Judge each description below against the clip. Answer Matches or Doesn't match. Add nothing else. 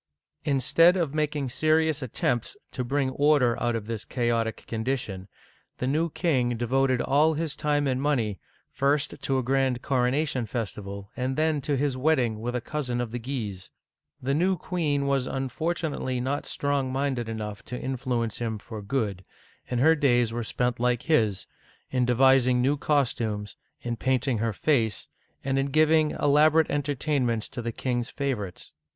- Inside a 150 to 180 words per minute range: Matches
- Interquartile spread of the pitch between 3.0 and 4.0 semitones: Matches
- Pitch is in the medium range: Doesn't match